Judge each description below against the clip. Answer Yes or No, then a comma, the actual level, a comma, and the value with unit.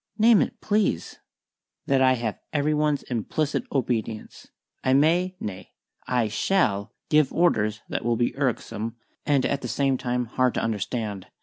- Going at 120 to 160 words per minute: Yes, average, 150 wpm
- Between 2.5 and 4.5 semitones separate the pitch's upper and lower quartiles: No, average, 5.1 semitones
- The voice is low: Yes, low, 130 Hz